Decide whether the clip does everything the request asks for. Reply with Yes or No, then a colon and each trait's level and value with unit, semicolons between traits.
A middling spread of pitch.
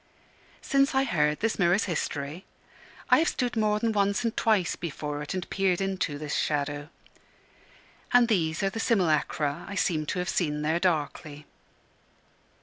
No: wide, 5.9 semitones